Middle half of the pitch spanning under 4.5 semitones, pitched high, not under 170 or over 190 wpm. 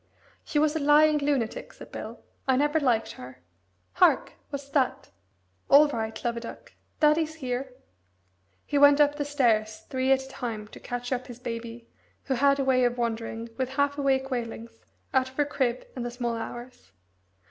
Yes: average, 3.2 semitones; very high, 260 Hz; average, 180 wpm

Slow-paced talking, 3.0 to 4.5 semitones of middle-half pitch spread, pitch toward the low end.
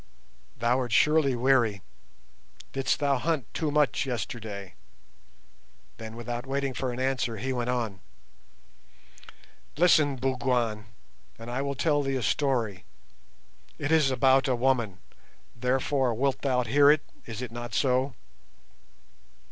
No: slow, 130 wpm; narrow, 2.6 semitones; low, 130 Hz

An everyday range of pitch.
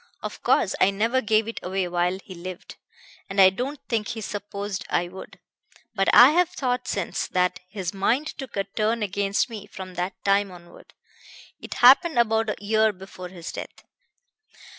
Yes: average, 3.4 semitones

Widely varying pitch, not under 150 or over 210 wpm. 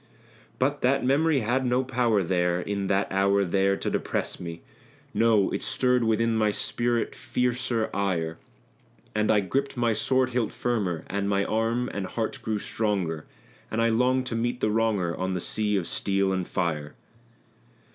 No: average, 3.9 semitones; average, 165 wpm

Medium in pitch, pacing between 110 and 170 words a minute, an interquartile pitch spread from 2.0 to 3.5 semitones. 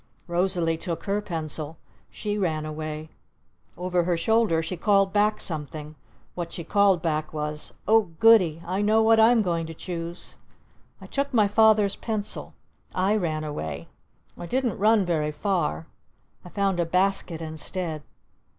No: medium, 180 Hz; average, 150 wpm; average, 4.5 semitones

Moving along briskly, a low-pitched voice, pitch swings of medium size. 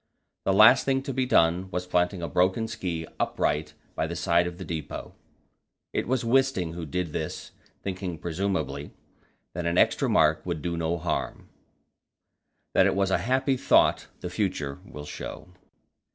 No: average, 165 wpm; very low, 90 Hz; average, 3.4 semitones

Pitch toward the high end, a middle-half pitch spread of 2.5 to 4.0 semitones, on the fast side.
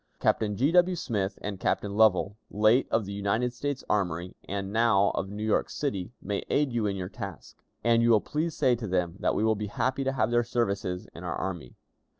No: low, 105 Hz; average, 3.5 semitones; fast, 215 wpm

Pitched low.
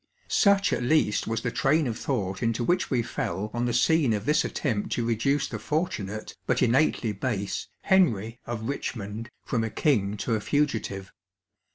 Yes: low, 115 Hz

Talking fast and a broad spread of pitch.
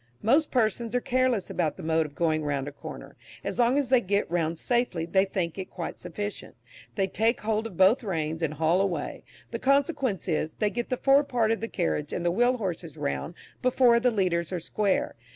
Yes: fast, 210 wpm; wide, 6.2 semitones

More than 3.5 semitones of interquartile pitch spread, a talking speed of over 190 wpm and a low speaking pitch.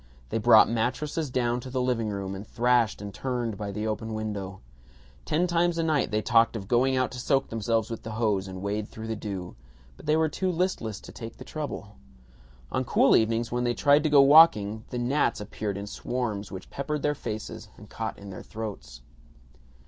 Yes: average, 4.0 semitones; fast, 205 wpm; low, 115 Hz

